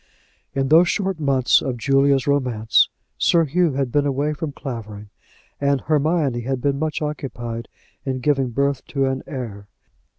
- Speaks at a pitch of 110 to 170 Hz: Yes, low, 135 Hz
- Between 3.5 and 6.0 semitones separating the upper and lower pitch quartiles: No, average, 2.8 semitones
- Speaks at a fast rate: No, average, 155 wpm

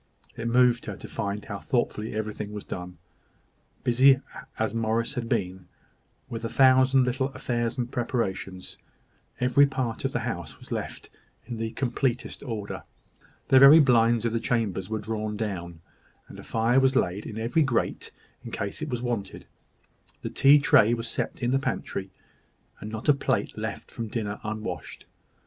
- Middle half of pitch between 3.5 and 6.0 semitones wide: No, average, 3.1 semitones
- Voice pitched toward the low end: Yes, low, 115 Hz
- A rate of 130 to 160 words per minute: No, average, 170 wpm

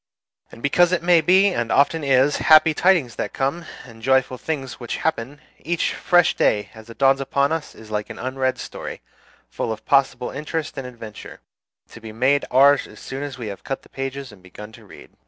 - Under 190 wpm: No, fast, 205 wpm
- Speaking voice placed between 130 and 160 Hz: Yes, low, 135 Hz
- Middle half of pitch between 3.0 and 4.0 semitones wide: No, average, 4.5 semitones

